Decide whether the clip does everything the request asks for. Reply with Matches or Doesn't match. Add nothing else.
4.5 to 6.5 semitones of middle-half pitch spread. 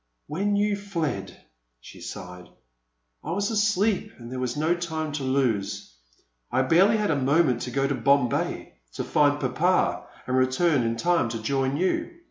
Matches